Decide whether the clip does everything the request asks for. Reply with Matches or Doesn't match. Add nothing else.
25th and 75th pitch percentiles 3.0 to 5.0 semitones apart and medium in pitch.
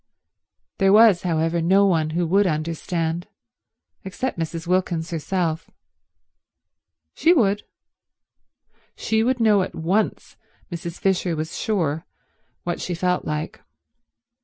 Matches